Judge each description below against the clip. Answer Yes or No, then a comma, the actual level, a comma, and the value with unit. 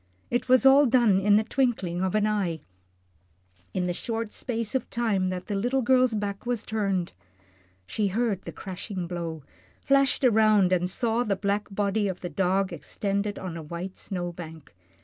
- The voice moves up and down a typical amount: Yes, average, 3.9 semitones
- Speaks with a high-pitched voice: Yes, high, 200 Hz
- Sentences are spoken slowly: No, average, 175 wpm